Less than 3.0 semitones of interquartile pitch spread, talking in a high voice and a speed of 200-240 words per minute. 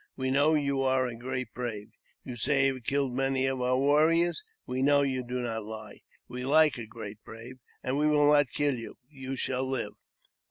No: narrow, 2.4 semitones; low, 130 Hz; fast, 205 wpm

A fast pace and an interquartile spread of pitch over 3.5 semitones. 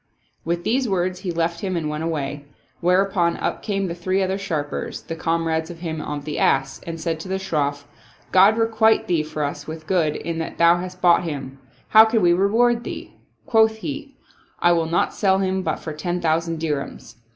No: fast, 215 wpm; average, 3.2 semitones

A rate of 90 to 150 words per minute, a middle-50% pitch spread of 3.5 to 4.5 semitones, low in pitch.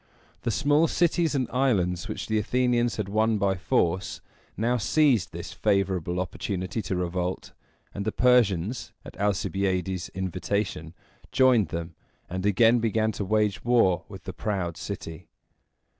Yes: average, 140 wpm; average, 4.2 semitones; low, 100 Hz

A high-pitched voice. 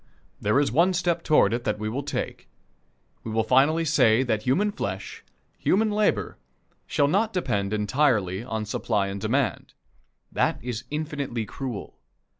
No: low, 130 Hz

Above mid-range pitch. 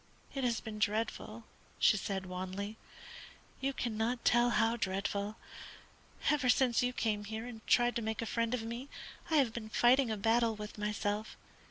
Yes: high, 225 Hz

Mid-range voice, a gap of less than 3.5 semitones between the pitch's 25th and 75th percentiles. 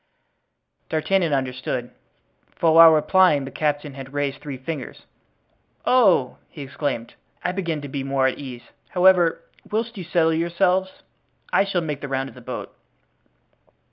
No: medium, 150 Hz; average, 4.6 semitones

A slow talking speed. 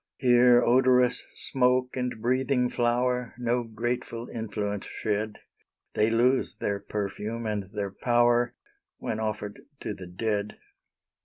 Yes: slow, 100 wpm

